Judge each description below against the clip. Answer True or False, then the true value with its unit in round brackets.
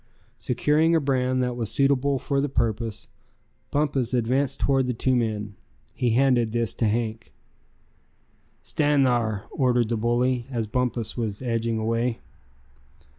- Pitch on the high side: False (120 Hz)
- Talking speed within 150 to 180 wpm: False (135 wpm)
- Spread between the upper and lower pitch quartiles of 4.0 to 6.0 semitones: False (2.5 semitones)